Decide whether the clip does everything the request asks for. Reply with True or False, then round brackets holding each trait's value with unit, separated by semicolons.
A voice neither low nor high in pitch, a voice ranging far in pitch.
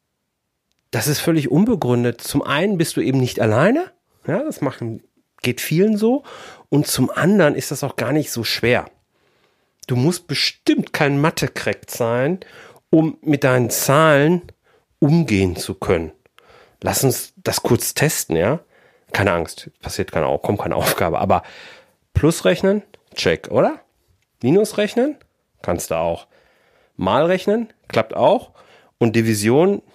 True (150 Hz; 7.6 semitones)